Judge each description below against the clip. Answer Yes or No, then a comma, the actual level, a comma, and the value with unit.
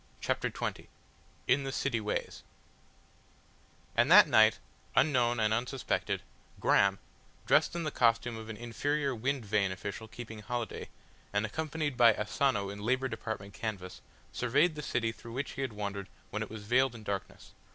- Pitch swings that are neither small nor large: Yes, average, 4.0 semitones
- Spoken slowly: No, average, 160 wpm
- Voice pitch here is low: Yes, low, 115 Hz